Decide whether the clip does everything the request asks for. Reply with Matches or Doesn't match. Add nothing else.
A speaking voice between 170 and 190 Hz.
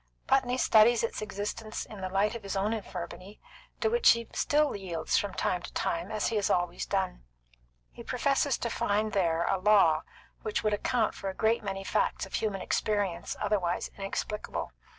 Doesn't match